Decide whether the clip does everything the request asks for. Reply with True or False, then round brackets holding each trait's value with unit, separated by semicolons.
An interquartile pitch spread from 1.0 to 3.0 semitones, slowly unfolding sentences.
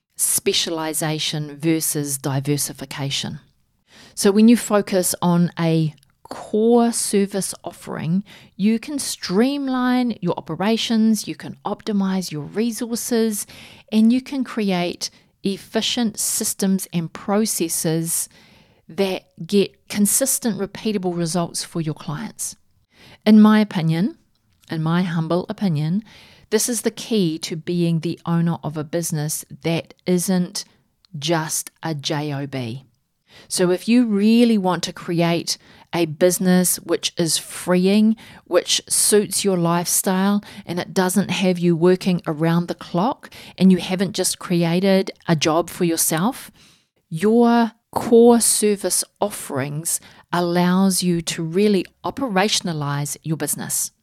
False (4.1 semitones; 120 wpm)